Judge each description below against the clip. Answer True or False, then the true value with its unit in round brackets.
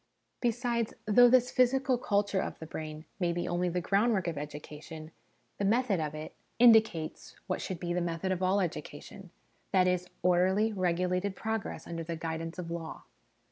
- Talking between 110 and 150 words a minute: False (180 wpm)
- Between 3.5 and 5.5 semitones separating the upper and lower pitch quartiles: True (4.2 semitones)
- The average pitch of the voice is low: False (180 Hz)